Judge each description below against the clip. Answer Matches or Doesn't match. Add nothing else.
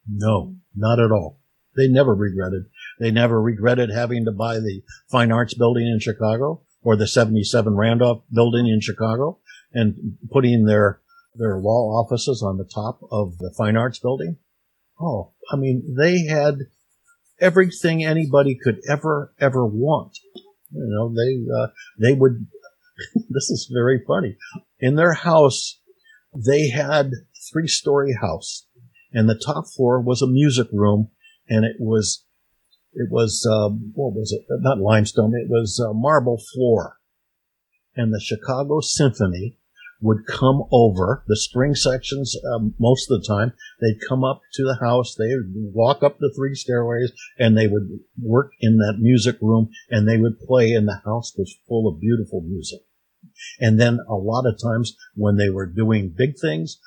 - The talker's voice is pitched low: Matches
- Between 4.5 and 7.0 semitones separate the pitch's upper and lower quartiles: Doesn't match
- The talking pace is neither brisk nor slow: Matches